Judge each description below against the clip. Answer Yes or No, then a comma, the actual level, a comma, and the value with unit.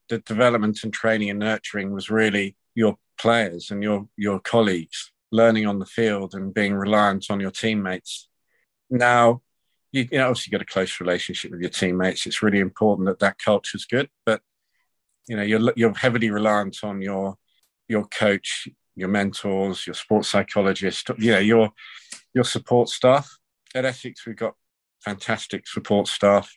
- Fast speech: No, average, 165 wpm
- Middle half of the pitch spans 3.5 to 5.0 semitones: No, average, 2.7 semitones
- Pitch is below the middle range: Yes, low, 105 Hz